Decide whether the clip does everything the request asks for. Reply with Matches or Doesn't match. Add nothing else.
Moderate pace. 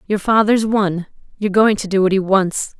Matches